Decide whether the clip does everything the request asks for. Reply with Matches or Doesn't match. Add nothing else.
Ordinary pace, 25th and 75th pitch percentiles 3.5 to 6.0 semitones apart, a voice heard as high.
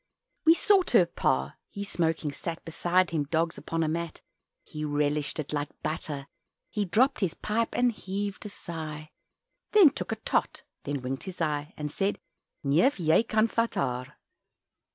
Doesn't match